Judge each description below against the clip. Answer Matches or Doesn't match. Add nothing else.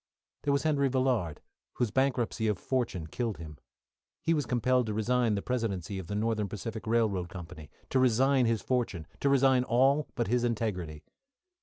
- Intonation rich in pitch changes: Doesn't match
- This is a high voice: Doesn't match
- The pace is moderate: Matches